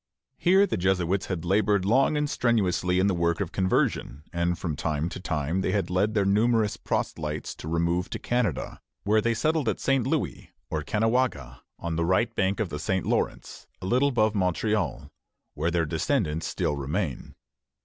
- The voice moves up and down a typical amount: Yes, average, 4.7 semitones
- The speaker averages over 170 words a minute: Yes, average, 180 wpm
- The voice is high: No, very low, 95 Hz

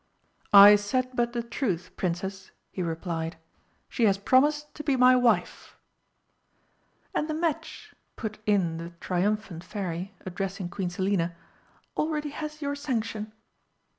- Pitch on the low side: No, high, 210 Hz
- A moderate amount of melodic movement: No, wide, 6.0 semitones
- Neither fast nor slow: No, slow, 130 wpm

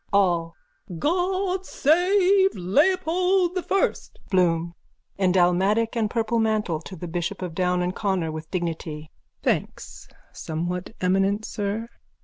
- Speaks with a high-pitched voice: Yes, high, 195 Hz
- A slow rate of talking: Yes, slow, 125 wpm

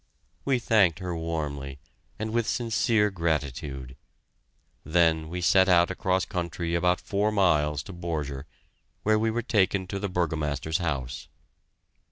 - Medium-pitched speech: No, very low, 85 Hz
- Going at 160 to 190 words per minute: No, slow, 135 wpm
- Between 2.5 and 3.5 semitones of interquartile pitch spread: No, average, 4.2 semitones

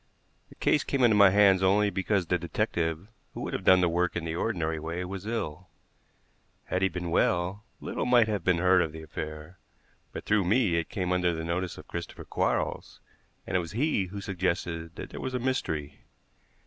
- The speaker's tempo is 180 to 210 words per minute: Yes, average, 200 wpm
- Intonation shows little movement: No, average, 3.3 semitones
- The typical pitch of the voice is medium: No, very low, 90 Hz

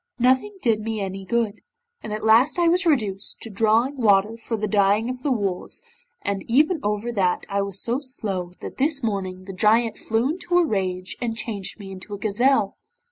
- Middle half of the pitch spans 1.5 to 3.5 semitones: No, average, 4.1 semitones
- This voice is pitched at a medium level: No, high, 220 Hz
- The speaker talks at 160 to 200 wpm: Yes, average, 195 wpm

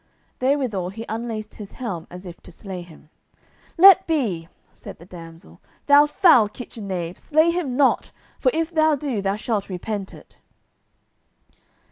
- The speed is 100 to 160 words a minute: Yes, average, 150 wpm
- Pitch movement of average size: No, wide, 8.1 semitones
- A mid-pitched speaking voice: No, high, 215 Hz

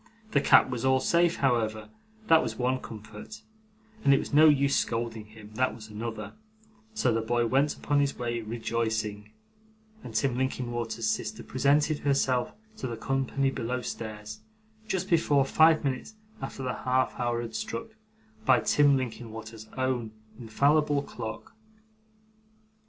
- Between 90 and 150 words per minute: Yes, average, 140 wpm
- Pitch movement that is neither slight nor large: Yes, average, 3.7 semitones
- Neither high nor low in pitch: No, low, 125 Hz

